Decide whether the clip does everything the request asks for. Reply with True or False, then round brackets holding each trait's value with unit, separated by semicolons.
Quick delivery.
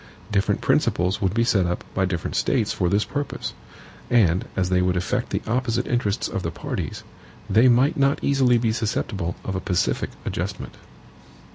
False (170 wpm)